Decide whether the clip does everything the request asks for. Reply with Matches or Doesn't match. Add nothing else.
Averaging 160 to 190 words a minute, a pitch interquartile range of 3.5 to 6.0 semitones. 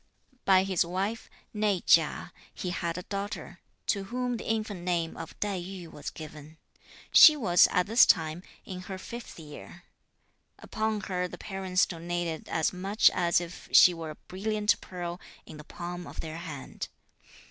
Doesn't match